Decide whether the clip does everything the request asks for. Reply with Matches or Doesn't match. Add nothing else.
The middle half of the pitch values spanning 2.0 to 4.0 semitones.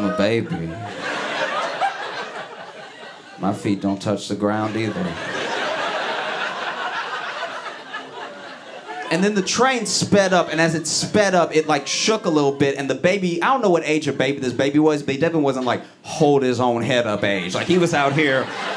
Doesn't match